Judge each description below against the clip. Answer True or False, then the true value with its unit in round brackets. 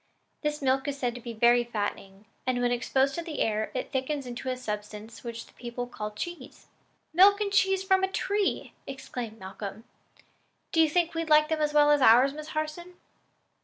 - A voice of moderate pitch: False (265 Hz)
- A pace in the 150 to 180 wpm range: False (195 wpm)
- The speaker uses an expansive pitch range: False (5.0 semitones)